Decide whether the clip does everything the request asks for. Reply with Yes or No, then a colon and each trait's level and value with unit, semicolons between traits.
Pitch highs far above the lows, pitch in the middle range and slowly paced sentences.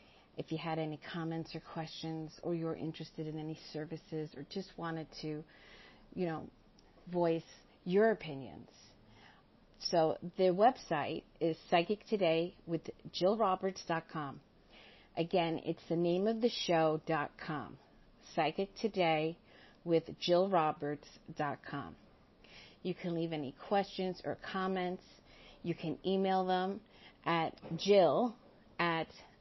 No: average, 2.7 semitones; medium, 165 Hz; slow, 110 wpm